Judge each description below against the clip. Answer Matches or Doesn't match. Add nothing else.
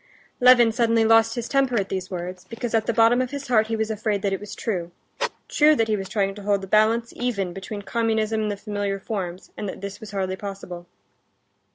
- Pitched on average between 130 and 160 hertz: Doesn't match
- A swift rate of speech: Matches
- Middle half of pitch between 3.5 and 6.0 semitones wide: Doesn't match